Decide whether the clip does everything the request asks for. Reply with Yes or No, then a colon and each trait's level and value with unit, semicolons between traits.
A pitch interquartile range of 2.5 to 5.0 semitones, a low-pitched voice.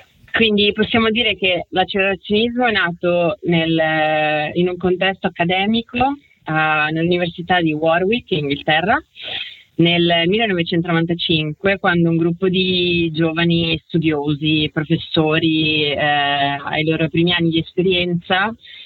No: average, 2.8 semitones; medium, 170 Hz